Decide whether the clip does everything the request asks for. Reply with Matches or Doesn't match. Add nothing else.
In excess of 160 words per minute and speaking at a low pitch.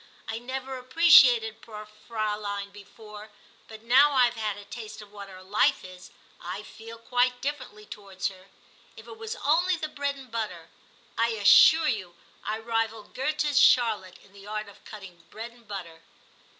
Doesn't match